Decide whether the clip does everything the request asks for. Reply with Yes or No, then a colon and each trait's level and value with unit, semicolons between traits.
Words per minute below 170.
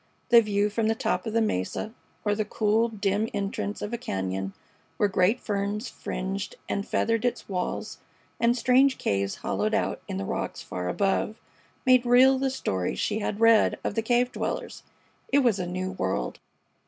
No: average, 180 wpm